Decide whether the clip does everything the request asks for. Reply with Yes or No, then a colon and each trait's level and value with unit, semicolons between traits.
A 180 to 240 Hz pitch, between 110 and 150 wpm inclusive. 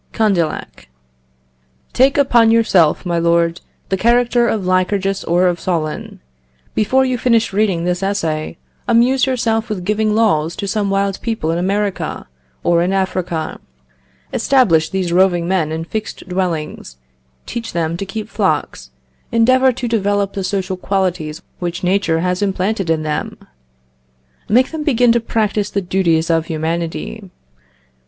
Yes: high, 190 Hz; average, 140 wpm